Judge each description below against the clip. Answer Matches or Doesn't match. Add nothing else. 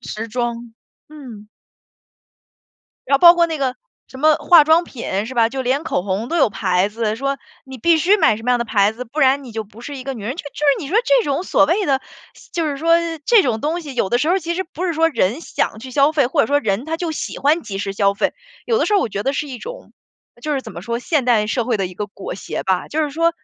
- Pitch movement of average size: Doesn't match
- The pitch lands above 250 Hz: Matches